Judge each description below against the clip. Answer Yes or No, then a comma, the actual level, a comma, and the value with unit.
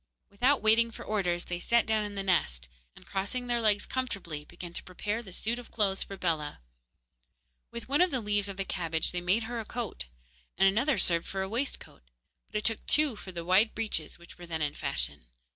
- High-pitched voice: Yes, high, 200 Hz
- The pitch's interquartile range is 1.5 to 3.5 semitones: No, average, 4.7 semitones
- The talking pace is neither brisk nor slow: No, fast, 215 wpm